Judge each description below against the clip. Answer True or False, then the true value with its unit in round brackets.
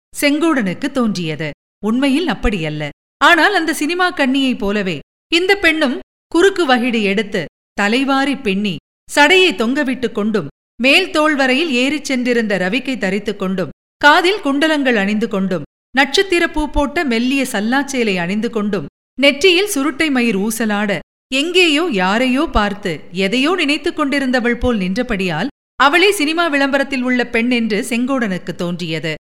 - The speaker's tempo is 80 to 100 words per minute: False (115 wpm)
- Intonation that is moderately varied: False (6.3 semitones)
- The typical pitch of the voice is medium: False (255 Hz)